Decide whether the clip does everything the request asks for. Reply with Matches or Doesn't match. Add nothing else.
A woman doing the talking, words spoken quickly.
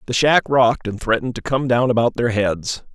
Doesn't match